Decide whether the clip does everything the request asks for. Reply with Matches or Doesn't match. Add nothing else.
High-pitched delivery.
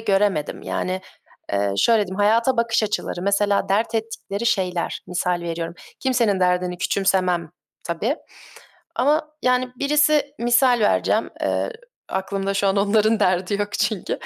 Matches